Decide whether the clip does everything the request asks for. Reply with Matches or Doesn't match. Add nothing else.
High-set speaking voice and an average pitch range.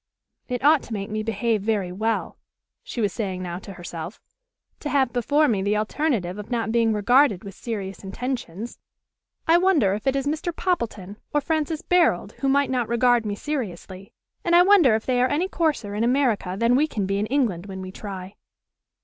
Doesn't match